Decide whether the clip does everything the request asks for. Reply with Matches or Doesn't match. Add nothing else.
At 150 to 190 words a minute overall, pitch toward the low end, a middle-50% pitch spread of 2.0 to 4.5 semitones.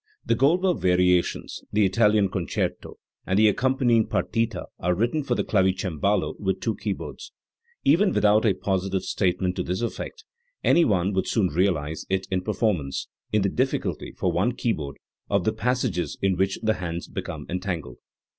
Matches